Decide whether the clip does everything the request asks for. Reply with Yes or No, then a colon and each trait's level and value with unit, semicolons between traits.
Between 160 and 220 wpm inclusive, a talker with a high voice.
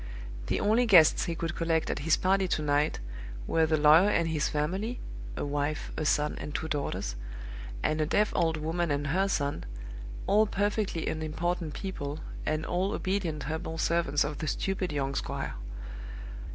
No: average, 165 wpm; medium, 160 Hz